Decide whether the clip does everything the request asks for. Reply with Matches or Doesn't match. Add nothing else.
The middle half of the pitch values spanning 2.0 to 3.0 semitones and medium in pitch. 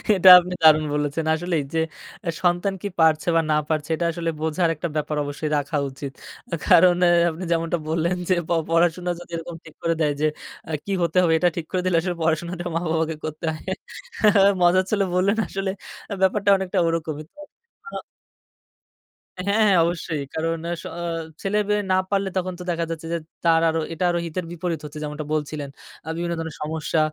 Matches